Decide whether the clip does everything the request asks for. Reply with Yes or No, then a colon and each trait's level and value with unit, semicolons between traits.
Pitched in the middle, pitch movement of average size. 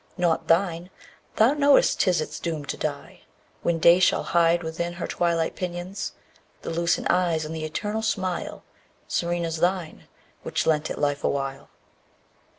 No: medium, 170 Hz; narrow, 2.0 semitones